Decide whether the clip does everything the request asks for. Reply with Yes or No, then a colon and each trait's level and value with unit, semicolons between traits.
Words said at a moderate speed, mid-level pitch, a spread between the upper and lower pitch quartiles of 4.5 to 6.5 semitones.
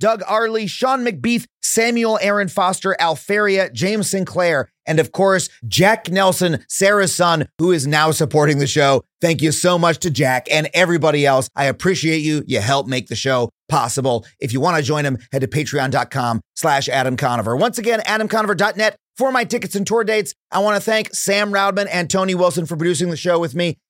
Yes: average, 195 wpm; medium, 175 Hz; average, 5.3 semitones